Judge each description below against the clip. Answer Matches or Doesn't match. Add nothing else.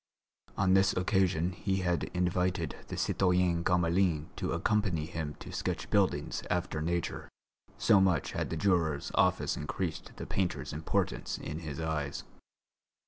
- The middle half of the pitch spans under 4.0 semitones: Matches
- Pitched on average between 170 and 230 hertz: Doesn't match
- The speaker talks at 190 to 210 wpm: Doesn't match